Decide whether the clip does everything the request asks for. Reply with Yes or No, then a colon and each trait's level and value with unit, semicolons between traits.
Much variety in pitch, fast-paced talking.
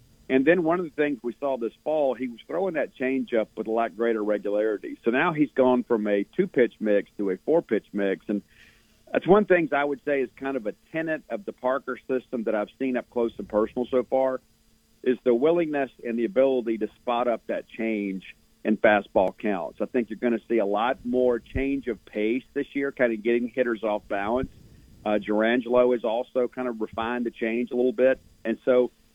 No: average, 3.0 semitones; fast, 220 wpm